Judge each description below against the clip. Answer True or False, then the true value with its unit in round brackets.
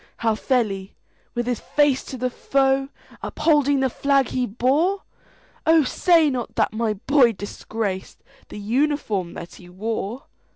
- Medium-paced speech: False (125 wpm)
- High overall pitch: True (250 Hz)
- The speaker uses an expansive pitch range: False (4.5 semitones)